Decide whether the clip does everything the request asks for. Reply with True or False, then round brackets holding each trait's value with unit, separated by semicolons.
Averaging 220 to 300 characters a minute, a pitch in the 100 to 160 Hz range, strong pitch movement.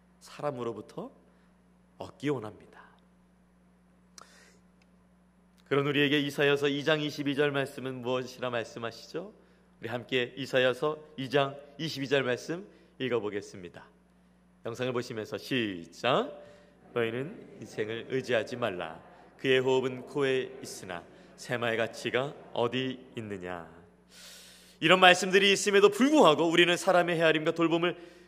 True (265 characters per minute; 135 Hz; 5.9 semitones)